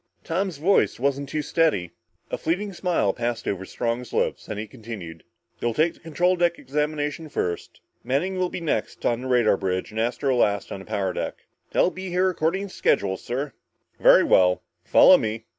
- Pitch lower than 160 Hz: Yes, low, 135 Hz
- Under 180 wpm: No, average, 185 wpm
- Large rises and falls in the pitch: Yes, wide, 7.8 semitones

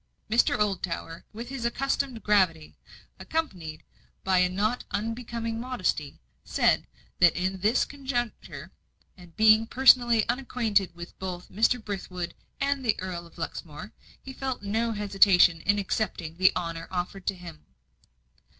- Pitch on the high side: Yes, high, 205 Hz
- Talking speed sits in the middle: No, slow, 130 wpm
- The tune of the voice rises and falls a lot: No, average, 4.7 semitones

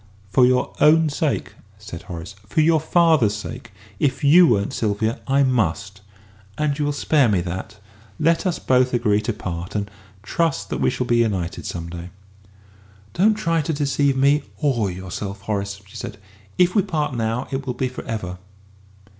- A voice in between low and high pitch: No, low, 125 Hz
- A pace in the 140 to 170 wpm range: No, average, 180 wpm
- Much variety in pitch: Yes, wide, 6.5 semitones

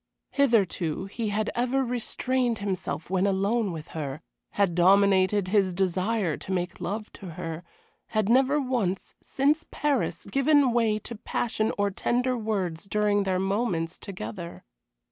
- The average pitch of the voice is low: No, high, 205 Hz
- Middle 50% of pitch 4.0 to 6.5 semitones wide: Yes, average, 4.4 semitones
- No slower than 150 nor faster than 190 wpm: No, average, 140 wpm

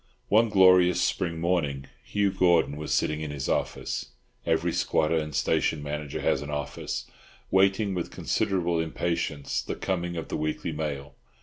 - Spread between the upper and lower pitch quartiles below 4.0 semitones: Yes, average, 3.6 semitones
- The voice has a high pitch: No, very low, 80 Hz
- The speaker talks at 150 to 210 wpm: No, average, 140 wpm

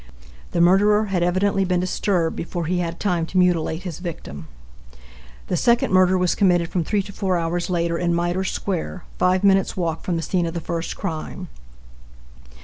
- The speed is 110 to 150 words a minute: No, average, 180 wpm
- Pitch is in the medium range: Yes, medium, 180 Hz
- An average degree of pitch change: No, narrow, 1.9 semitones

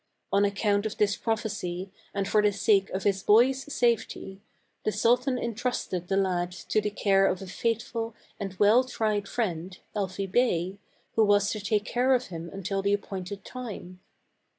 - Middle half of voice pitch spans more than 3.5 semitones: No, average, 2.7 semitones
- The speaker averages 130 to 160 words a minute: No, average, 170 wpm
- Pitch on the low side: No, high, 205 Hz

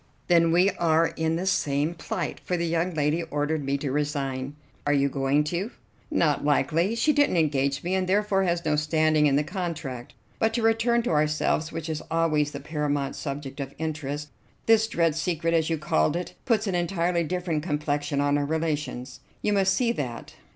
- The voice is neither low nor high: Yes, medium, 160 Hz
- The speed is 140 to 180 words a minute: No, average, 195 wpm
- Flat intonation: No, average, 3.2 semitones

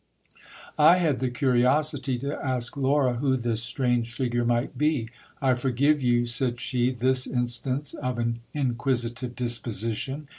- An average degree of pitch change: No, narrow, 2.3 semitones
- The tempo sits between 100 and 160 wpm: Yes, average, 140 wpm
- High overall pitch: No, low, 125 Hz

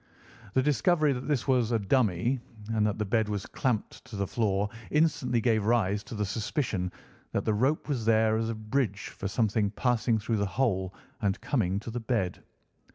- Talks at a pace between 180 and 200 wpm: Yes, average, 190 wpm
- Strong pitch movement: No, average, 3.4 semitones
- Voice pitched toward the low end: Yes, low, 110 Hz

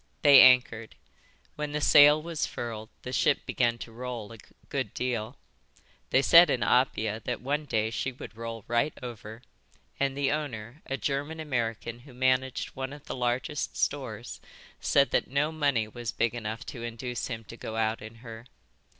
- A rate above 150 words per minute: Yes, average, 175 wpm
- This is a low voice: Yes, low, 125 Hz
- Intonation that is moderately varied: Yes, average, 3.5 semitones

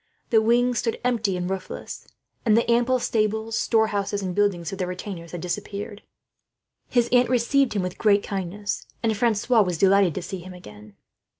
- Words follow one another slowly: No, average, 175 wpm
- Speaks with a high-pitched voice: Yes, high, 205 Hz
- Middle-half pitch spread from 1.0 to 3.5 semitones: No, average, 4.0 semitones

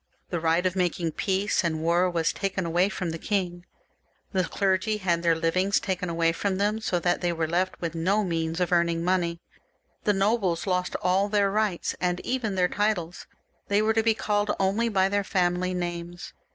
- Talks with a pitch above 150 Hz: Yes, medium, 185 Hz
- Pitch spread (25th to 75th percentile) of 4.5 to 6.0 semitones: No, average, 2.7 semitones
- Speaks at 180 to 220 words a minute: Yes, average, 190 wpm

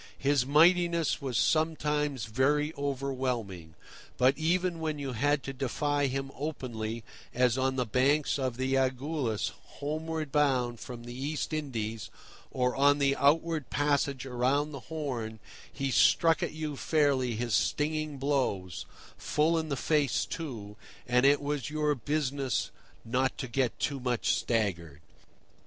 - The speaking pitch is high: No, medium, 140 Hz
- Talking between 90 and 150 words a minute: Yes, average, 140 wpm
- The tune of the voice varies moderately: Yes, average, 3.2 semitones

